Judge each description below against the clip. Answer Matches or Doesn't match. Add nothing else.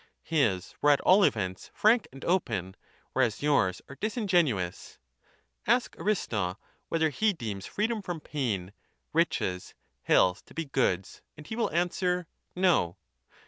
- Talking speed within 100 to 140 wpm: Matches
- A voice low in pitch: Doesn't match